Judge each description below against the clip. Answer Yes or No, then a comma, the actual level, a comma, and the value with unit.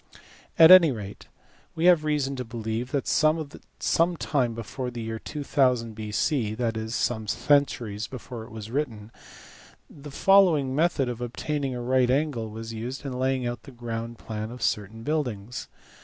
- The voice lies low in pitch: Yes, low, 125 Hz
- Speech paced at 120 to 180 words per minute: Yes, average, 160 wpm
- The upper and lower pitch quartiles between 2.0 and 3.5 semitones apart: No, average, 4.2 semitones